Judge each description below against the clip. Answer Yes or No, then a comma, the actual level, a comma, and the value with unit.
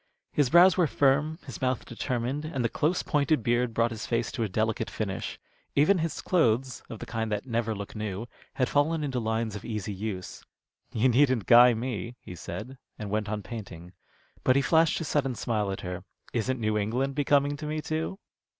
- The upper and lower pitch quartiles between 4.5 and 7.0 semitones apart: Yes, average, 4.8 semitones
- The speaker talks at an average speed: Yes, average, 195 wpm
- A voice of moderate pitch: No, low, 120 Hz